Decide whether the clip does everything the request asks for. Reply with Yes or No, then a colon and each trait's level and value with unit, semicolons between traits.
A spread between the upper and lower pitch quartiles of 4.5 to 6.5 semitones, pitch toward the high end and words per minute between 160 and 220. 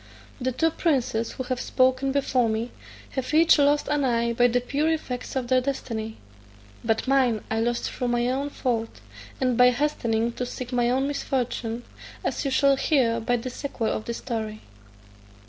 No: narrow, 2.6 semitones; very high, 250 Hz; average, 180 wpm